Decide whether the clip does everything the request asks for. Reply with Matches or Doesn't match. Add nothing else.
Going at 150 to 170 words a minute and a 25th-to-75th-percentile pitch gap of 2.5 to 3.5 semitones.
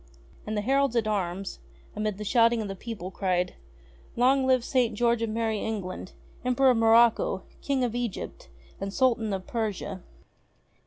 Matches